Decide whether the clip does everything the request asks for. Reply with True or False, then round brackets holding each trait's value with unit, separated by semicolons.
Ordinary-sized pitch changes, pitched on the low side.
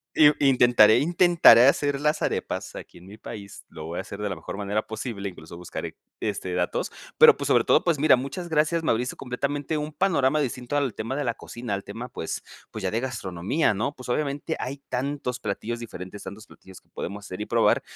False (6.0 semitones; 120 Hz)